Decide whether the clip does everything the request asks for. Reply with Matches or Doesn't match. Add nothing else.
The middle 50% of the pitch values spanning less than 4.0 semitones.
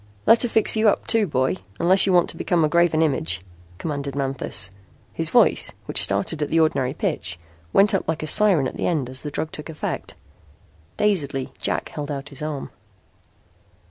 Doesn't match